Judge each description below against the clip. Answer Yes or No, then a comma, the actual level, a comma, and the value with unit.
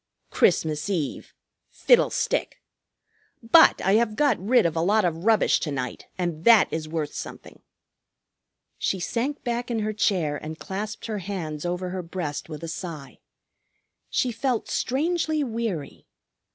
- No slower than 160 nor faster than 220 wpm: No, average, 145 wpm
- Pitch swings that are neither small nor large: No, wide, 6.2 semitones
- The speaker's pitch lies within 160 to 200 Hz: Yes, high, 190 Hz